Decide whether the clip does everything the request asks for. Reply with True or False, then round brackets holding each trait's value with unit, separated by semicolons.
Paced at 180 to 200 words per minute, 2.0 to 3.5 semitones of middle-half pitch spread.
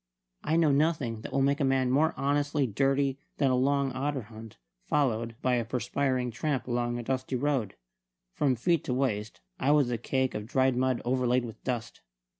True (190 wpm; 2.6 semitones)